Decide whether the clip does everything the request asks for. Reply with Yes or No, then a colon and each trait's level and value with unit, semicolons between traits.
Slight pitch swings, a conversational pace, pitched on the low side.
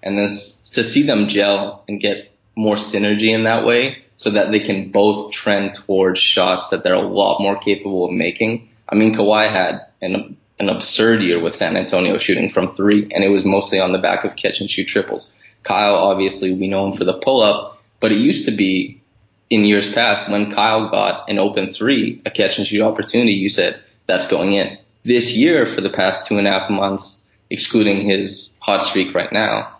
No: narrow, 1.8 semitones; fast, 210 wpm; low, 100 Hz